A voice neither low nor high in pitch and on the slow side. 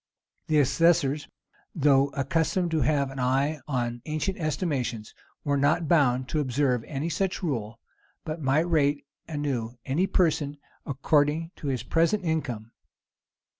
Yes: medium, 145 Hz; slow, 130 wpm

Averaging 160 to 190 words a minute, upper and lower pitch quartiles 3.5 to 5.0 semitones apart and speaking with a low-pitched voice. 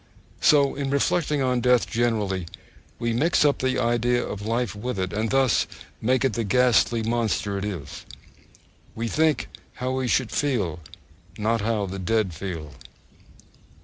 No: average, 150 wpm; average, 3.9 semitones; low, 115 Hz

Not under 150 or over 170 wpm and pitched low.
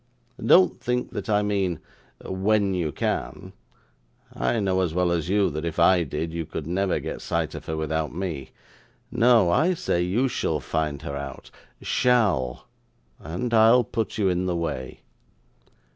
Yes: average, 160 wpm; very low, 90 Hz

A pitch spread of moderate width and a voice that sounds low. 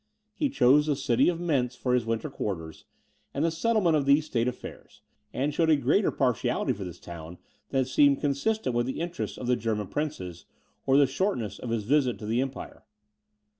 Yes: average, 4.7 semitones; low, 130 Hz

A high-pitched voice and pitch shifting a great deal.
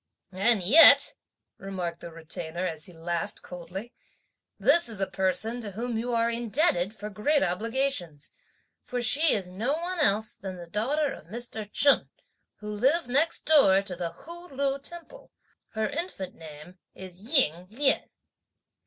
Yes: high, 215 Hz; wide, 7.1 semitones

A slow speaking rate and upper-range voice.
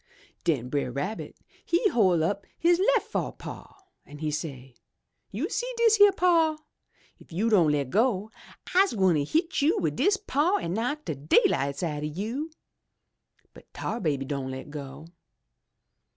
No: average, 160 wpm; high, 195 Hz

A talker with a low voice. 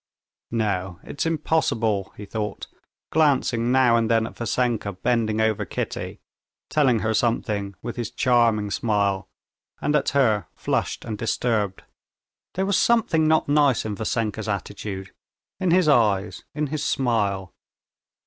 Yes: low, 115 Hz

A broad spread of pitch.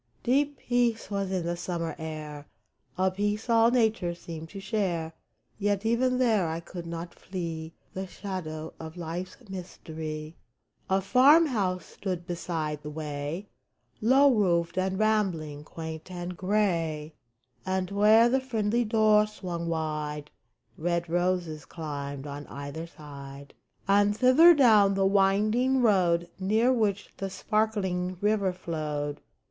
No: average, 4.8 semitones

